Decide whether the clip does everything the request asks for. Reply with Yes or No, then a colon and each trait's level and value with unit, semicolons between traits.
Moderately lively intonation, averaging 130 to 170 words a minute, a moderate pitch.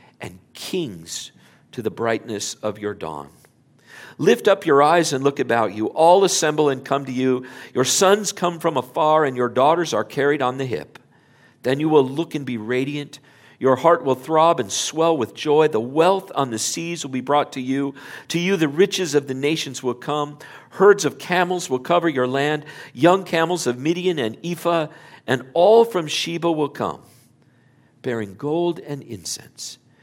No: average, 4.6 semitones; average, 185 wpm; medium, 145 Hz